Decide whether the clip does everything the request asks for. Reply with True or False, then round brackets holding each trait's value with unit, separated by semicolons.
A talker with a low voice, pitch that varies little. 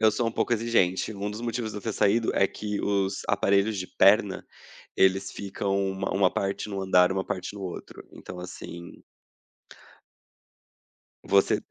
True (100 Hz; 1.9 semitones)